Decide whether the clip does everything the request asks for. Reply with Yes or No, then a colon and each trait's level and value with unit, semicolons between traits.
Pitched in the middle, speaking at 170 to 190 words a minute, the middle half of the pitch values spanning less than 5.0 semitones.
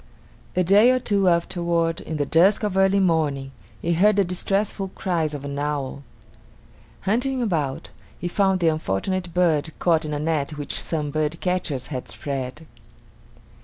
No: medium, 165 Hz; average, 155 wpm; average, 4.3 semitones